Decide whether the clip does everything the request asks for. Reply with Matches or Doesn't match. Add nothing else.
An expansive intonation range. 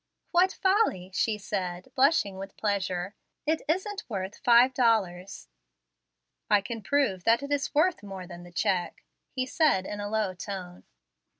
Matches